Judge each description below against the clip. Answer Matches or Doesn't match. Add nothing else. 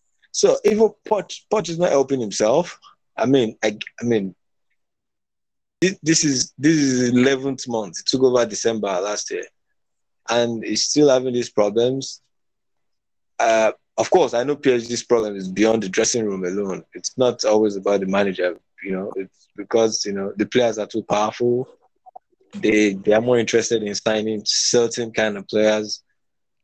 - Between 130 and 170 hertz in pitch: Doesn't match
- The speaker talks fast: Doesn't match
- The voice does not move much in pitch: Doesn't match